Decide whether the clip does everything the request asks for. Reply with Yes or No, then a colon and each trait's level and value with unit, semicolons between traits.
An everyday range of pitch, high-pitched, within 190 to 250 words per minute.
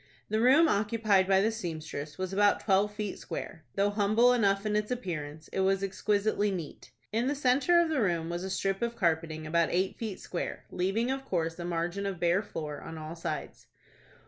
Yes: average, 4.2 semitones; high, 195 Hz; average, 200 wpm